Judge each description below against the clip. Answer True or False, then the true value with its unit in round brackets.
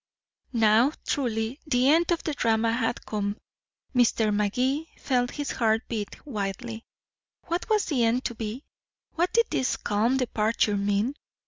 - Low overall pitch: False (235 Hz)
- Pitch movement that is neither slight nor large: True (3.9 semitones)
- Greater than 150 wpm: False (145 wpm)